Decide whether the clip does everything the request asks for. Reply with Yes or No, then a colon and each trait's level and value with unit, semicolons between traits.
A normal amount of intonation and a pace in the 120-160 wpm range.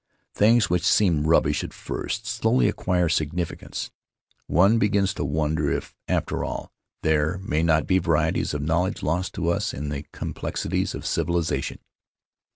Yes: average, 3.9 semitones; average, 155 wpm